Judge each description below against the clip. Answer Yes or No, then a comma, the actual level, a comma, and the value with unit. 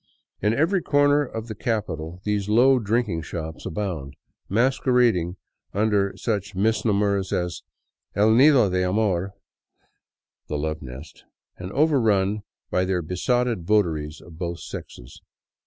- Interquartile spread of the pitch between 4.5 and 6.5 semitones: Yes, average, 4.8 semitones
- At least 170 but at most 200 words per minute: No, average, 145 wpm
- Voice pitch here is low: Yes, low, 100 Hz